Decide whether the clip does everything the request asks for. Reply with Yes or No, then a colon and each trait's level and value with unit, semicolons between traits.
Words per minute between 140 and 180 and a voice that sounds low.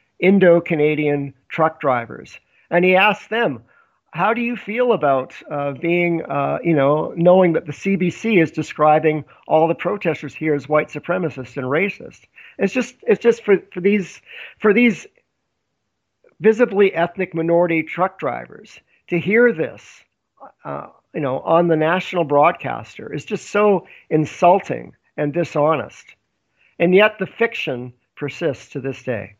No: average, 145 wpm; medium, 170 Hz